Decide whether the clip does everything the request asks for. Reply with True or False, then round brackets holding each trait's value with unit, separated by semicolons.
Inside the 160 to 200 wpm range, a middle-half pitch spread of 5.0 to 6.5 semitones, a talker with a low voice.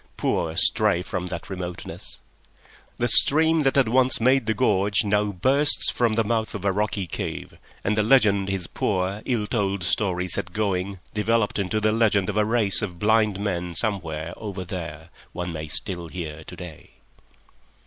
False (170 wpm; 3.5 semitones; 100 Hz)